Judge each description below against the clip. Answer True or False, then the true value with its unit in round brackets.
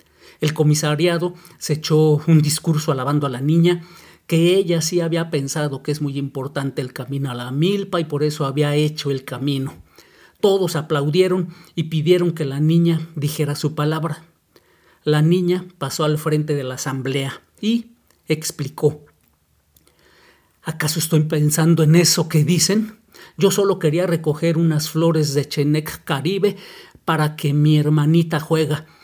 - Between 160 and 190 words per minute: False (150 wpm)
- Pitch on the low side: False (155 Hz)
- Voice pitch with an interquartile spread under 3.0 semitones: True (2.4 semitones)